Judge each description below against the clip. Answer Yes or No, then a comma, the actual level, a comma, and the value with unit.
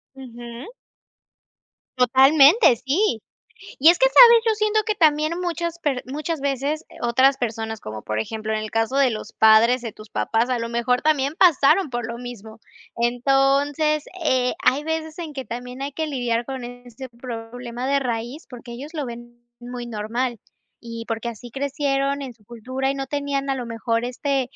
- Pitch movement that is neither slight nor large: Yes, average, 3.4 semitones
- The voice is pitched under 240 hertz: No, very high, 255 Hz